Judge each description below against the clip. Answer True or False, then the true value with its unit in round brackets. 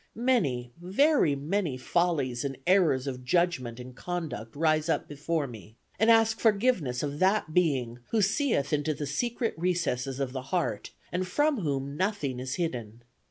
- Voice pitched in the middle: True (155 Hz)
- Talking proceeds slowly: False (160 wpm)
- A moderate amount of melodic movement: False (6.4 semitones)